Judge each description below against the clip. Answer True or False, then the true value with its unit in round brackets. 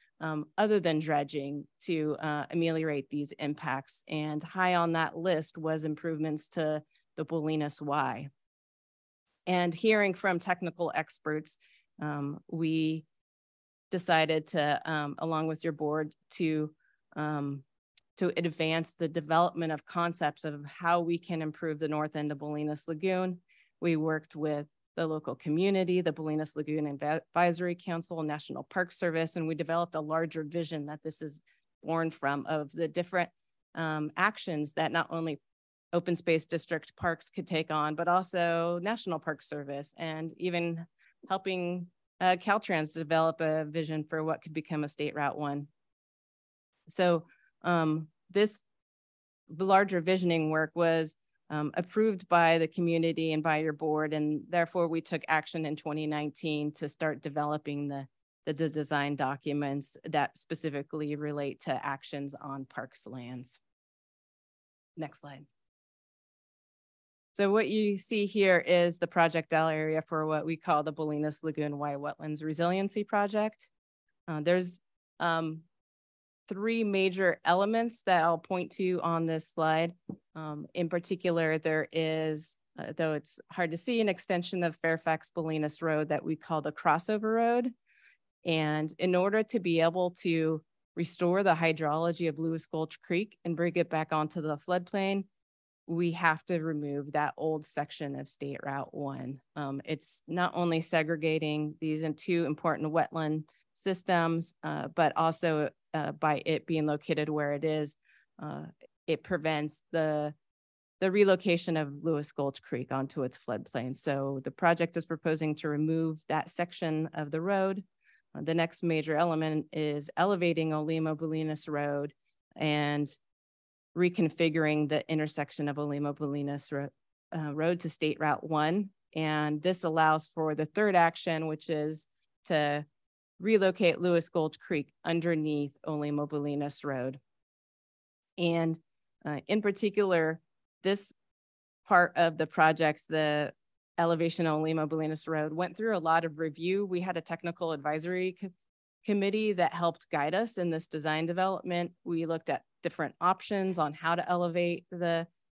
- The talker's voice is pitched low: False (160 Hz)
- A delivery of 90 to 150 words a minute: True (145 wpm)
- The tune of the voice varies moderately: False (2.2 semitones)